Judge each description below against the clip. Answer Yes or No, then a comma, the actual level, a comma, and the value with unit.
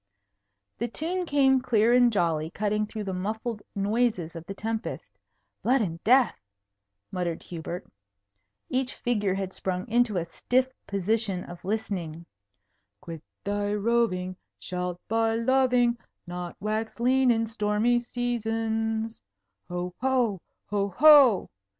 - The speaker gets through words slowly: Yes, slow, 125 wpm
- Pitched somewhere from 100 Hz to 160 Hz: No, high, 220 Hz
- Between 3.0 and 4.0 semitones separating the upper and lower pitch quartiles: No, average, 4.6 semitones